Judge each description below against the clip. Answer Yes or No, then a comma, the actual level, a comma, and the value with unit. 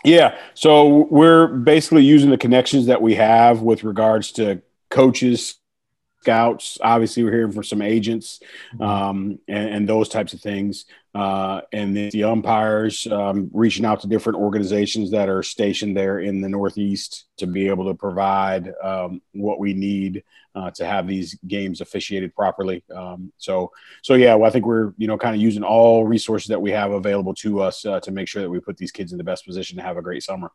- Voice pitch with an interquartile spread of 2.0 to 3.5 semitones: Yes, narrow, 2.5 semitones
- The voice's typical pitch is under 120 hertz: Yes, low, 105 Hz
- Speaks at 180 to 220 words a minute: Yes, average, 200 wpm